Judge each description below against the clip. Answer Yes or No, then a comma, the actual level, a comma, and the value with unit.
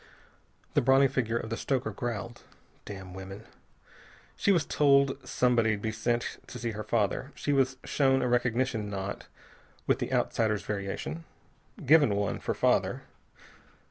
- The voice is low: Yes, low, 120 Hz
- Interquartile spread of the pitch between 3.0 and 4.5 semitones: Yes, average, 4.0 semitones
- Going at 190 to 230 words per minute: No, average, 140 wpm